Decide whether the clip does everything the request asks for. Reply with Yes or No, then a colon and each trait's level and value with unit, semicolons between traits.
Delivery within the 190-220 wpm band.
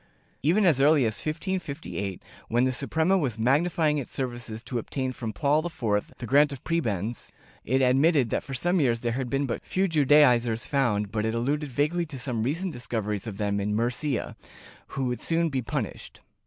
Yes: average, 195 wpm